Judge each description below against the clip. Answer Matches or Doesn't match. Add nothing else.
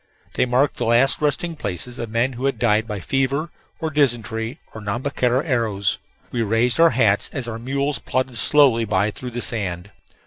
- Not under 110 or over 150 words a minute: Doesn't match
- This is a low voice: Matches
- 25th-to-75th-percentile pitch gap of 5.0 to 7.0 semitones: Doesn't match